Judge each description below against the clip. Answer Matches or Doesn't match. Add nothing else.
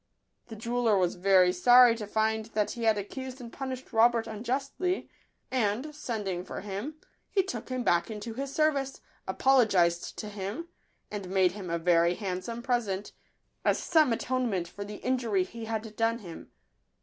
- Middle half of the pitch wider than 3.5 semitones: Matches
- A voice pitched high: Matches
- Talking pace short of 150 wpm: Doesn't match